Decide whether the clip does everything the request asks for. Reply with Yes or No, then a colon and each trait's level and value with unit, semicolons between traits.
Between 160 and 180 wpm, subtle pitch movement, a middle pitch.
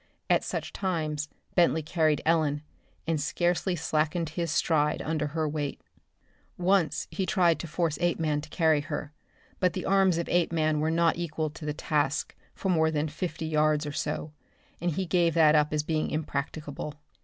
Yes: average, 170 wpm; narrow, 2.1 semitones; medium, 160 Hz